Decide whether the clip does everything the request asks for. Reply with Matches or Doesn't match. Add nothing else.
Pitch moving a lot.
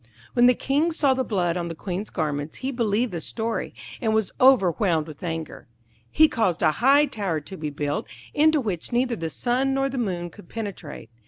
Matches